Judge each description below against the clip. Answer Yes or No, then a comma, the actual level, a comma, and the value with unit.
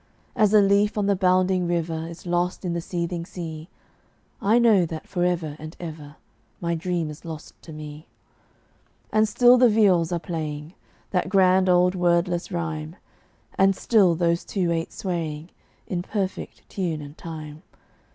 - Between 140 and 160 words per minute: Yes, average, 155 wpm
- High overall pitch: No, medium, 175 Hz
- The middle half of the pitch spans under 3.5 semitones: Yes, narrow, 2.6 semitones